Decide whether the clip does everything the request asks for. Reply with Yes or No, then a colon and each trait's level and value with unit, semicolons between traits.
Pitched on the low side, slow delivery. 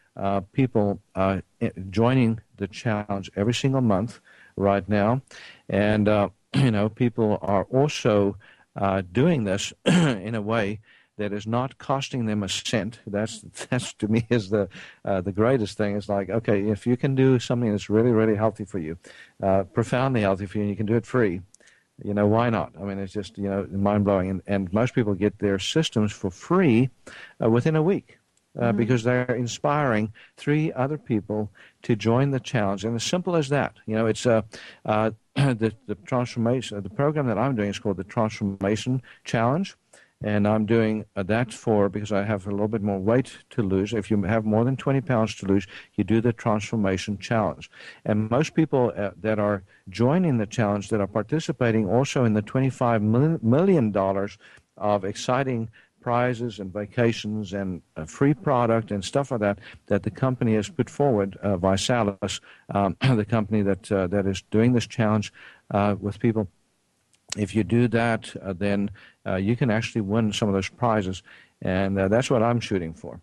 No: low, 110 Hz; average, 185 wpm